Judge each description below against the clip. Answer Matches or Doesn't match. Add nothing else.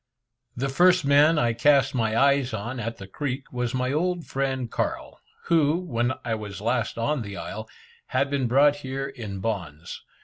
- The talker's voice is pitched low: Matches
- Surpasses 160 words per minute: Matches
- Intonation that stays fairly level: Doesn't match